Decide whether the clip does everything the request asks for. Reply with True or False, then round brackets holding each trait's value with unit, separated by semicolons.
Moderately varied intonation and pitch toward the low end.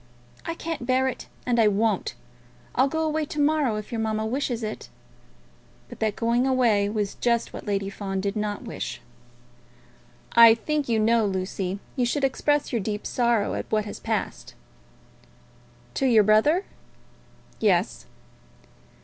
False (3.8 semitones; 230 Hz)